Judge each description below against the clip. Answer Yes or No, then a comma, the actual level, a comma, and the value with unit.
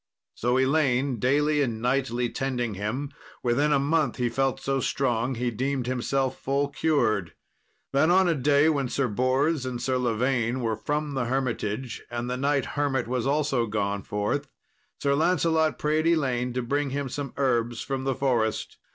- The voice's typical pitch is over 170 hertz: No, low, 130 Hz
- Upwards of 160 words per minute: Yes, average, 170 wpm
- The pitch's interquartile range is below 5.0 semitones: Yes, average, 2.8 semitones